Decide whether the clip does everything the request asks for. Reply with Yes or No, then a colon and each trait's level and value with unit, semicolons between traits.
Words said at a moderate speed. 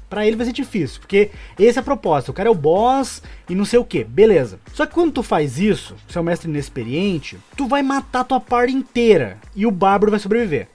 No: fast, 235 wpm